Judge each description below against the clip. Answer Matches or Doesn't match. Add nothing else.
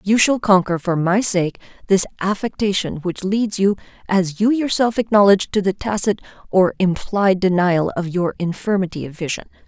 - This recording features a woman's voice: Matches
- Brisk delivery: Doesn't match